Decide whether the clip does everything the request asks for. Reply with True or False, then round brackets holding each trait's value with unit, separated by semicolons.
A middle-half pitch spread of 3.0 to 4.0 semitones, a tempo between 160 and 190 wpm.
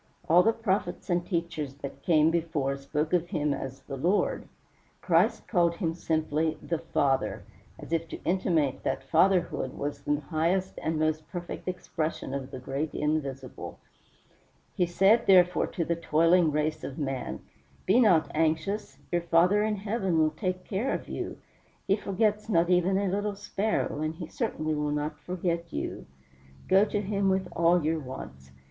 True (3.6 semitones; 165 wpm)